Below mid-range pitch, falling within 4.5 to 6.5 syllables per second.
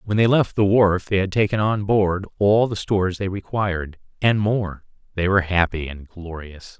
Yes: very low, 95 Hz; 4.8 syllables/s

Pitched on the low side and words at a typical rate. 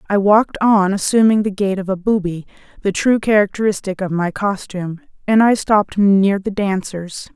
No: high, 200 Hz; average, 170 wpm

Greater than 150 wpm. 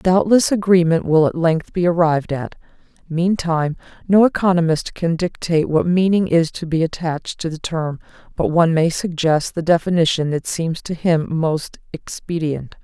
Yes: average, 160 wpm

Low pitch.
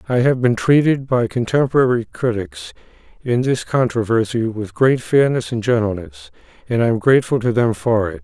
Yes: low, 120 Hz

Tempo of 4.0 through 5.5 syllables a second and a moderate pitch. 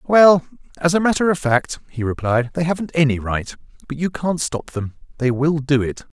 Yes: 5.0 syllables/s; medium, 150 Hz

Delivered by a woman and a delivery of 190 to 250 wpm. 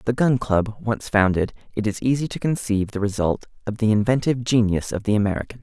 No: male; fast, 205 wpm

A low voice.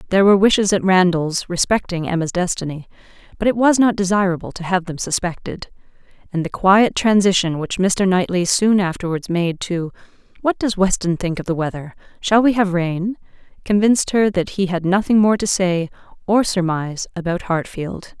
No: medium, 185 Hz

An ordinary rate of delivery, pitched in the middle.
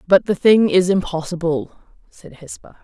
Yes: average, 150 wpm; medium, 180 Hz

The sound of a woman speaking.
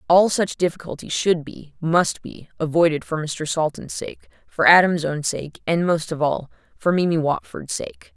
Yes: female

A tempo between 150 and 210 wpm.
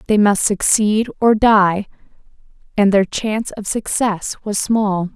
No: average, 140 wpm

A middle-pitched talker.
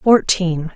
Yes: medium, 175 Hz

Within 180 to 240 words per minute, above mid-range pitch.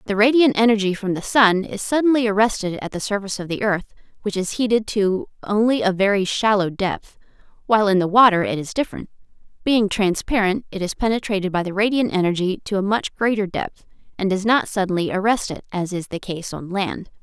Yes: average, 200 wpm; high, 200 Hz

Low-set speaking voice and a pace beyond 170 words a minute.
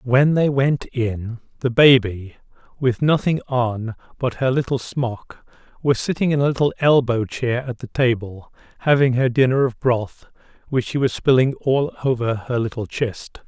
No: low, 125 Hz; average, 165 wpm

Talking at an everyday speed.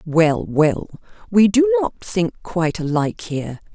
Yes: average, 145 wpm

